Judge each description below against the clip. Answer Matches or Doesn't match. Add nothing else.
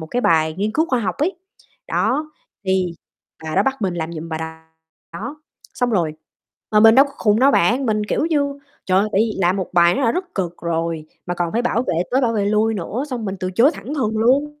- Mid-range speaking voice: Doesn't match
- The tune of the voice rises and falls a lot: Matches